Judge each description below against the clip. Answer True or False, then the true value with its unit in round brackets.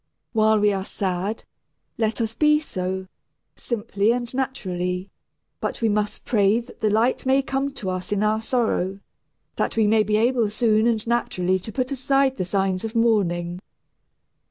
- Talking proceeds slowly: False (165 wpm)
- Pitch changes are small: False (3.6 semitones)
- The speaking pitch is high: True (215 Hz)